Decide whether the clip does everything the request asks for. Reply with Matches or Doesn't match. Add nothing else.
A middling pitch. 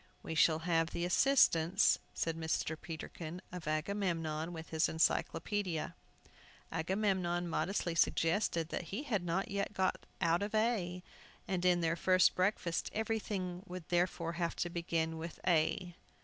Matches